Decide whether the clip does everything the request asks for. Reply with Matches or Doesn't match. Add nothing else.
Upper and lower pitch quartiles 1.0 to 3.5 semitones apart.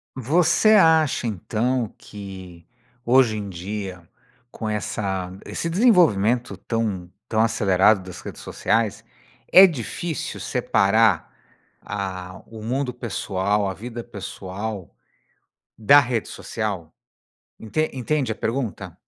Doesn't match